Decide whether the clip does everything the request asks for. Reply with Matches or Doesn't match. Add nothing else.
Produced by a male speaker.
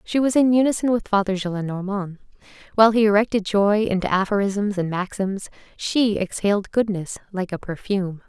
Doesn't match